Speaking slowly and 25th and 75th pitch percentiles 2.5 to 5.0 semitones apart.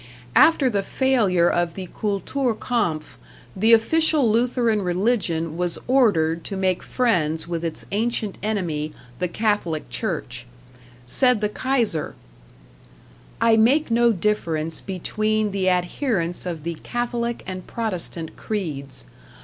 No: slow, 120 wpm; wide, 5.5 semitones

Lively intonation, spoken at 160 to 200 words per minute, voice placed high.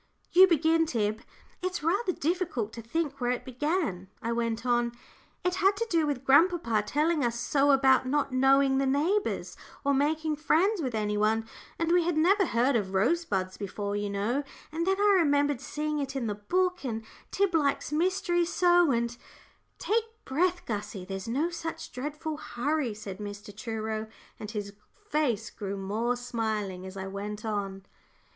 Yes: wide, 7.1 semitones; average, 170 wpm; very high, 270 Hz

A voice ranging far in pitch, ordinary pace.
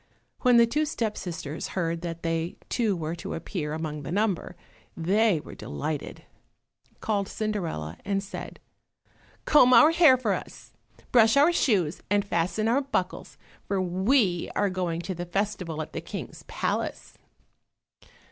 No: average, 5.0 semitones; average, 145 wpm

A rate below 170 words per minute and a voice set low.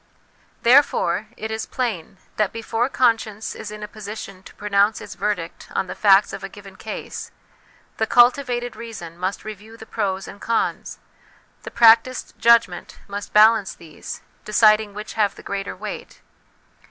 No: average, 155 wpm; high, 215 Hz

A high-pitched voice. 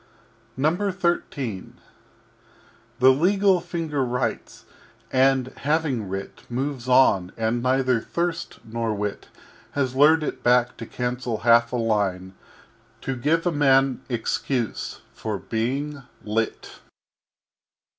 No: low, 130 Hz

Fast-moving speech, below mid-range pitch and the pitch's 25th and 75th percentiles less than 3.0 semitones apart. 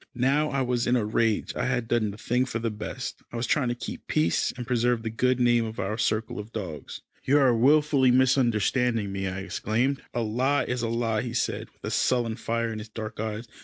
Yes: fast, 230 wpm; low, 120 Hz; narrow, 2.5 semitones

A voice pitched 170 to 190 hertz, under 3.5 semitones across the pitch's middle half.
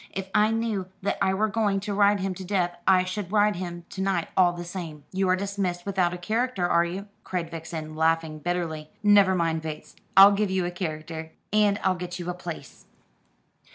Yes: medium, 185 Hz; average, 2.7 semitones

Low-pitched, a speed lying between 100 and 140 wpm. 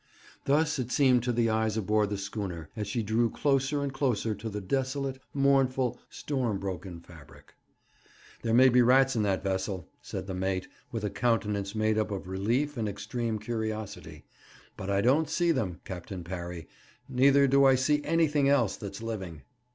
No: low, 110 Hz; average, 175 wpm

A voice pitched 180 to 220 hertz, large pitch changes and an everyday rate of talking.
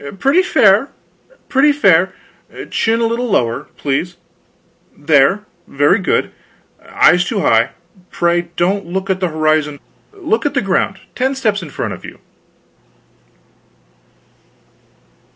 No: high, 190 Hz; wide, 6.5 semitones; slow, 120 wpm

